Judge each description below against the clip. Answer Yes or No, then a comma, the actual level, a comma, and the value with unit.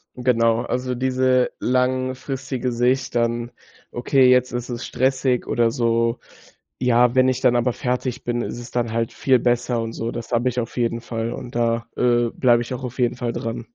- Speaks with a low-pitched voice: Yes, low, 120 Hz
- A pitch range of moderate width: No, narrow, 1.5 semitones